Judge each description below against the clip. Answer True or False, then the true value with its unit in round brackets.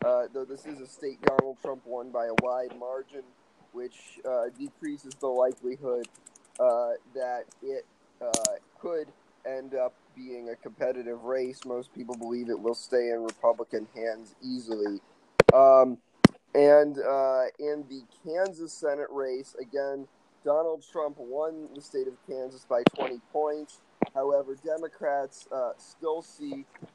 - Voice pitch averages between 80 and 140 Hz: True (135 Hz)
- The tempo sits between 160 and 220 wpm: False (140 wpm)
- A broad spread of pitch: False (3.7 semitones)